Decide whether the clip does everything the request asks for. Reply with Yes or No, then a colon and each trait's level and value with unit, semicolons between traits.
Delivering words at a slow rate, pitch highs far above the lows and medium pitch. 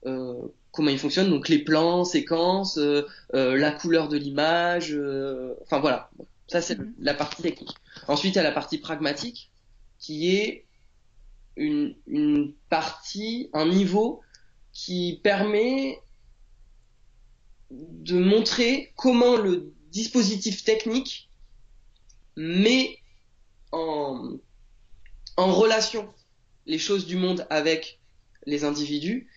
Yes: slow, 110 wpm; wide, 6.9 semitones; medium, 165 Hz